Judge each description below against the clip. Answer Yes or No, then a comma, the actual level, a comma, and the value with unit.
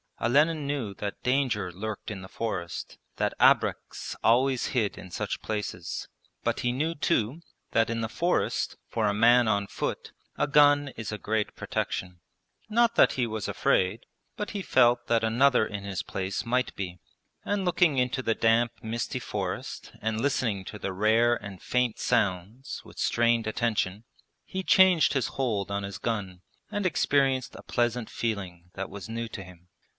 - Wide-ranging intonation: No, average, 4.3 semitones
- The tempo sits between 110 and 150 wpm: No, average, 170 wpm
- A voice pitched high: No, low, 115 Hz